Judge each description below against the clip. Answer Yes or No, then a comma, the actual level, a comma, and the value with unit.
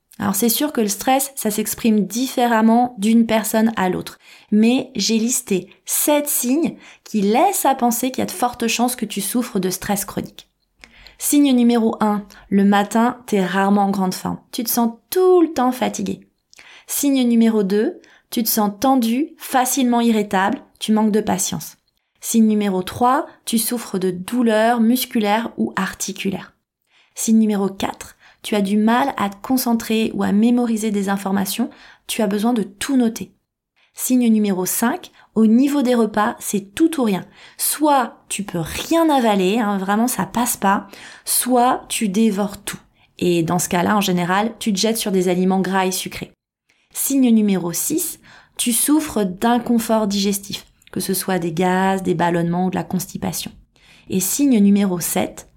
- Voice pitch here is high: Yes, high, 220 Hz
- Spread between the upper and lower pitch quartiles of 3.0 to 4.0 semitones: Yes, average, 3.7 semitones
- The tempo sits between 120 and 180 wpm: Yes, average, 170 wpm